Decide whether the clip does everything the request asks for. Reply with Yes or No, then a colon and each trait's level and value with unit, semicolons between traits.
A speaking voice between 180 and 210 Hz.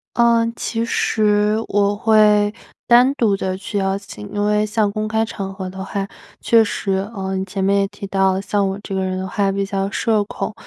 Yes: high, 200 Hz